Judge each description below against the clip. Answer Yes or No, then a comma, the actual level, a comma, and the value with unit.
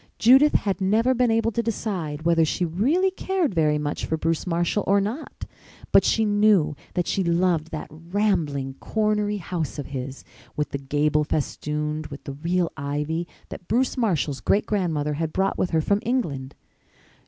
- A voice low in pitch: No, medium, 170 Hz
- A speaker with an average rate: Yes, average, 170 wpm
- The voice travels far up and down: Yes, wide, 5.7 semitones